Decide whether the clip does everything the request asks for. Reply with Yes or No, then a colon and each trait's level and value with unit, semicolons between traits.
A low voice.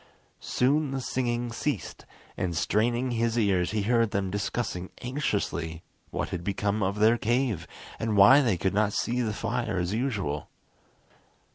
Yes: low, 110 Hz